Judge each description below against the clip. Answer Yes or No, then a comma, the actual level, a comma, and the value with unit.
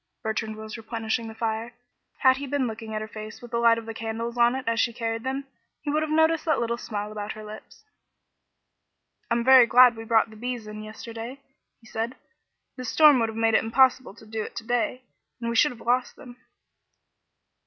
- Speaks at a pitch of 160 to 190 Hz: No, high, 230 Hz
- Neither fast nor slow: No, fast, 215 wpm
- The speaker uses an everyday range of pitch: No, narrow, 2.2 semitones